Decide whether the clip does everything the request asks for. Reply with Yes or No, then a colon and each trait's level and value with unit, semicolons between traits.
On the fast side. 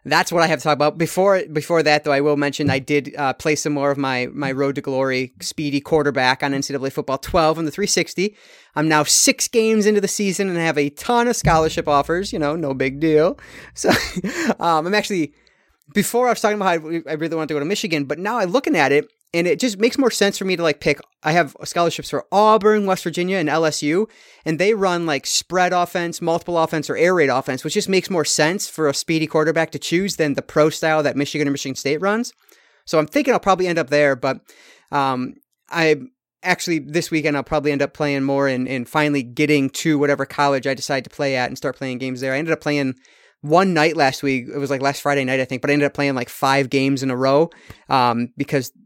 Yes: fast, 240 wpm